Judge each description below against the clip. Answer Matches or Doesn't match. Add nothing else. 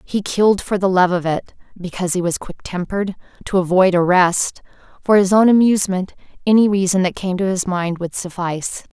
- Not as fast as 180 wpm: Matches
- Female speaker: Matches